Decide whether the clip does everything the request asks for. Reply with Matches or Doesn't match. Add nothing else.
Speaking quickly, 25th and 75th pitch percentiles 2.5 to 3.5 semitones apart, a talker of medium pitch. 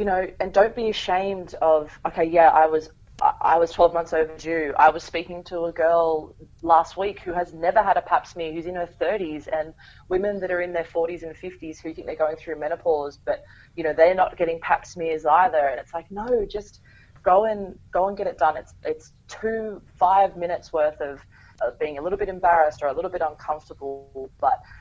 Matches